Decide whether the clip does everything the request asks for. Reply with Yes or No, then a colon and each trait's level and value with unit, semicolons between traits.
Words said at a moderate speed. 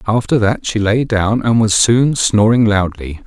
Yes: average, 185 wpm